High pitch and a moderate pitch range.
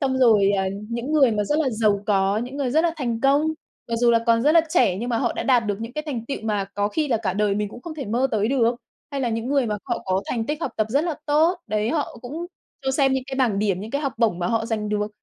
Yes: high, 235 Hz; average, 4.5 semitones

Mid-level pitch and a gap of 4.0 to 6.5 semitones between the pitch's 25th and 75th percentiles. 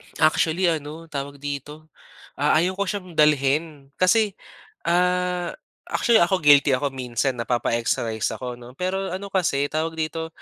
Yes: medium, 155 Hz; average, 4.5 semitones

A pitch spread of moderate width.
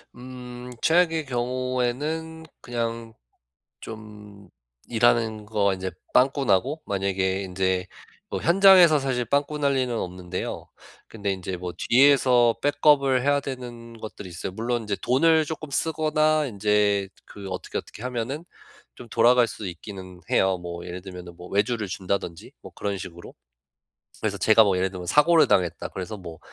No: wide, 5.9 semitones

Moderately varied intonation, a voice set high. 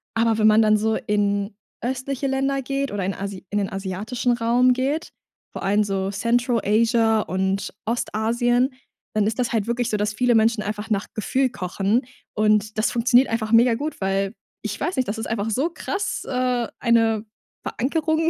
Yes: average, 3.1 semitones; high, 225 Hz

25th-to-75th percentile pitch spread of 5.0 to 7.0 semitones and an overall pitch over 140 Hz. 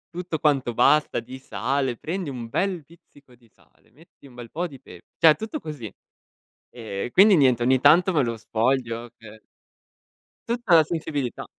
No: wide, 5.4 semitones; low, 135 Hz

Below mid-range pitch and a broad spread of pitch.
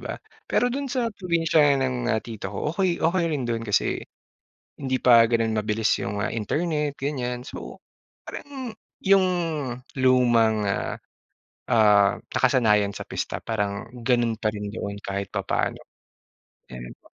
Yes: low, 120 Hz; wide, 6.3 semitones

